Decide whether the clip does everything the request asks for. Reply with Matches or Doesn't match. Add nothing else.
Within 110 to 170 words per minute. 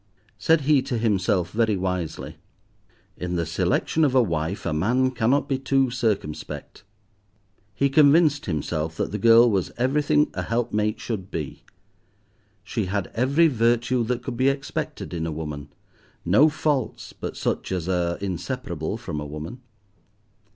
Matches